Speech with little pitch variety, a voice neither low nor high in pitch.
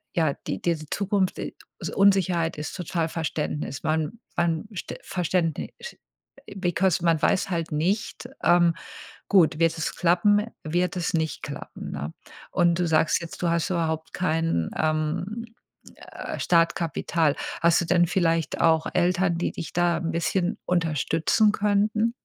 Yes: narrow, 2.2 semitones; medium, 170 Hz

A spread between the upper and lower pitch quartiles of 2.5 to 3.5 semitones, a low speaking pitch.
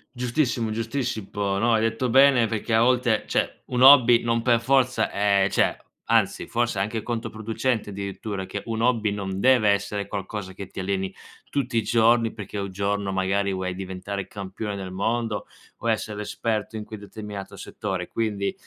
Yes: average, 2.8 semitones; low, 110 Hz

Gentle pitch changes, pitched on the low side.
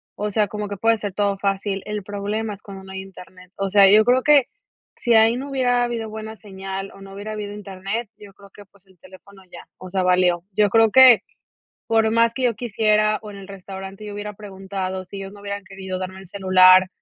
No: narrow, 2.1 semitones; high, 200 Hz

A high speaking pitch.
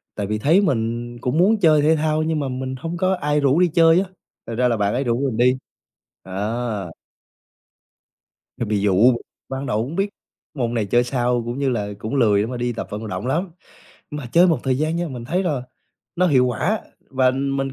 No: low, 130 Hz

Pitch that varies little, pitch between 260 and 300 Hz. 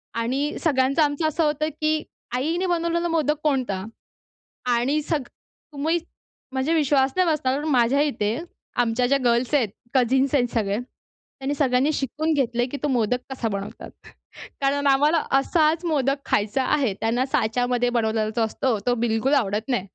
No: average, 3.8 semitones; very high, 265 Hz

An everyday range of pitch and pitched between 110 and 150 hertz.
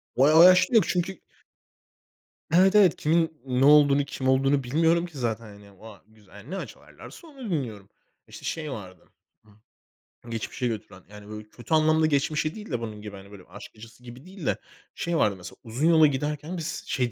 No: wide, 6.9 semitones; low, 135 Hz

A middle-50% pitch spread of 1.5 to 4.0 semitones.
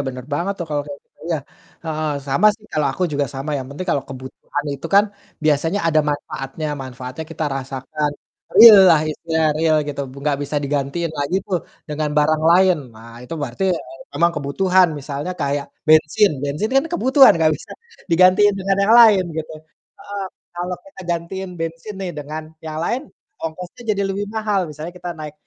No: average, 4.6 semitones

